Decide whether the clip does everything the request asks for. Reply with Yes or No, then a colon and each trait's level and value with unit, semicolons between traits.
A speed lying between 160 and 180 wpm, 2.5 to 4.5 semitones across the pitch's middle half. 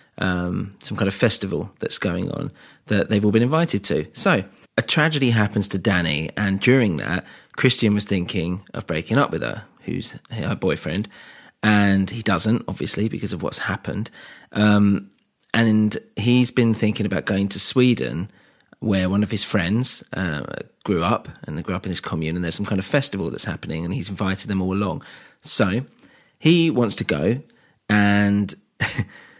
Yes: average, 175 wpm; average, 2.9 semitones